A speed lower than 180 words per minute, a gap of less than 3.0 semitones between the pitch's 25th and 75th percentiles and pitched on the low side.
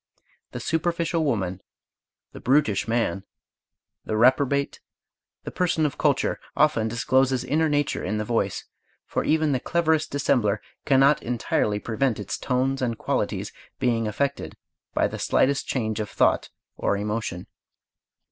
No: slow, 135 wpm; average, 5.0 semitones; low, 130 Hz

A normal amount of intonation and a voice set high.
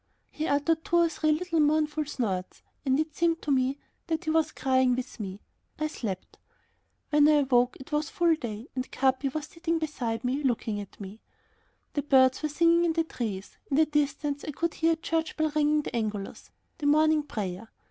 Yes: average, 3.7 semitones; very high, 295 Hz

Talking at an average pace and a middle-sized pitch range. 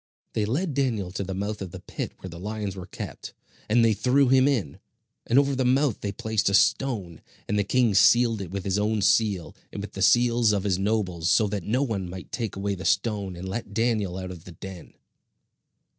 No: fast, 220 wpm; average, 3.6 semitones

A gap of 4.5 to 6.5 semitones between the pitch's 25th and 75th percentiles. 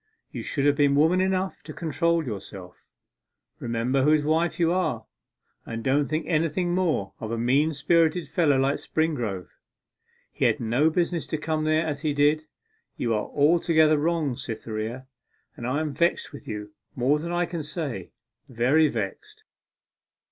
Yes: average, 4.9 semitones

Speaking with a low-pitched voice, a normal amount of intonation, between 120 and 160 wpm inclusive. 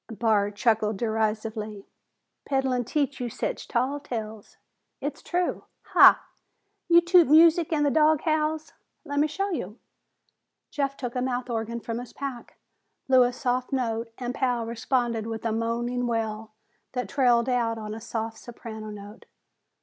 No: high, 240 Hz; average, 3.7 semitones; average, 150 wpm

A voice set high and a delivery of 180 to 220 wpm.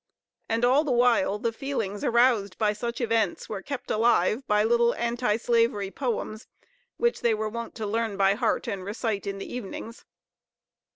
No: high, 225 Hz; average, 170 wpm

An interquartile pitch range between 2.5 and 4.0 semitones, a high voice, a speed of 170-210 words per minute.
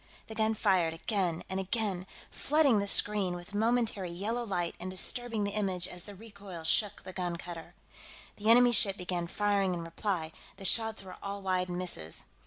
Yes: average, 3.2 semitones; high, 195 Hz; average, 180 wpm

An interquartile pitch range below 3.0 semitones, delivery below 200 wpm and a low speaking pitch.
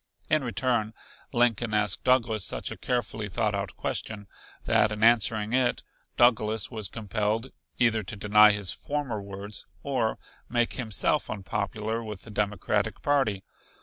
Yes: narrow, 2.4 semitones; average, 140 wpm; low, 110 Hz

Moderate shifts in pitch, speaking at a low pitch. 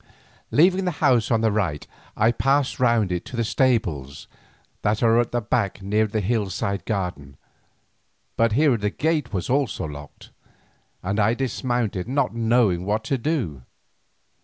Yes: average, 4.3 semitones; low, 110 Hz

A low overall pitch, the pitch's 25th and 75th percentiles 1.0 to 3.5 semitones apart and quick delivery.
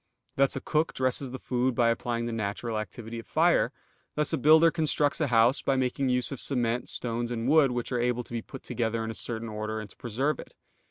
Yes: low, 120 Hz; average, 2.7 semitones; fast, 230 wpm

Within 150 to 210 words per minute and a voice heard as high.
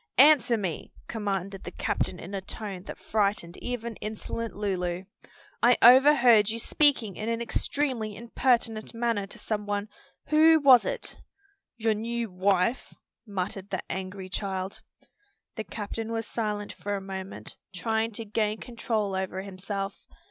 No: average, 140 wpm; high, 215 Hz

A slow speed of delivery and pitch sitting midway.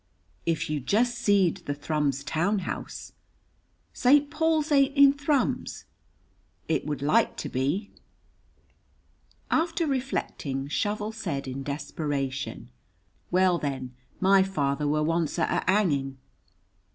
Yes: slow, 115 wpm; medium, 165 Hz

